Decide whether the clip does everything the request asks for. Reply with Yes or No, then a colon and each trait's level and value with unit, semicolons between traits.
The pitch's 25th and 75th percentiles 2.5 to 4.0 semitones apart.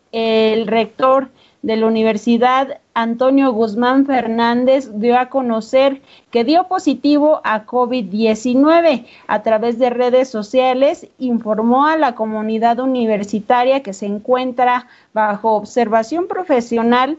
Yes: average, 3.0 semitones